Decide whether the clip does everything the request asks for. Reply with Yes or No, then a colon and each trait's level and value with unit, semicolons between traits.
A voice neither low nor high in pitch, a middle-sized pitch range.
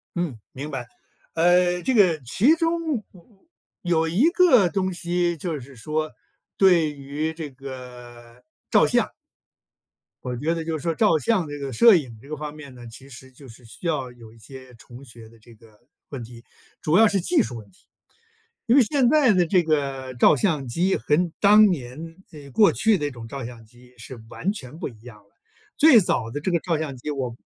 No: medium, 150 Hz; wide, 6.2 semitones